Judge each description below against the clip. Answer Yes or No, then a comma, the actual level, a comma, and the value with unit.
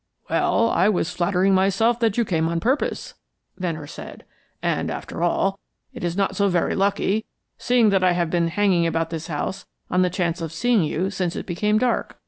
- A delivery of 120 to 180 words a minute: No, average, 195 wpm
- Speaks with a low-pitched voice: No, medium, 185 Hz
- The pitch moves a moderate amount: Yes, average, 3.4 semitones